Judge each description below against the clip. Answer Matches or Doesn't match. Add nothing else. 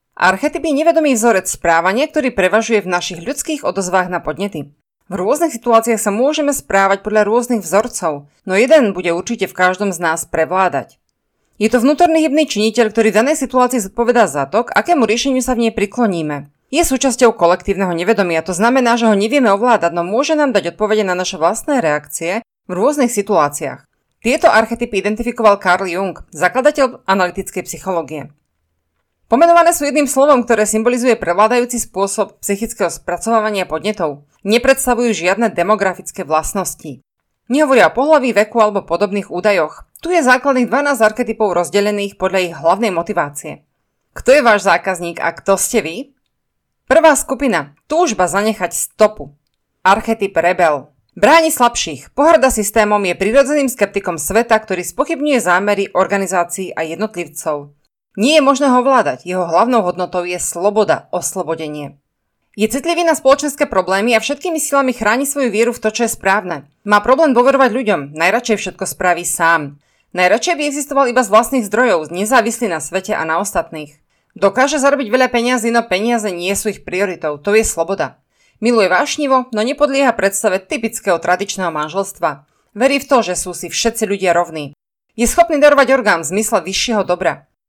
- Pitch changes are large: Matches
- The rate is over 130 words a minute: Matches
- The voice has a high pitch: Matches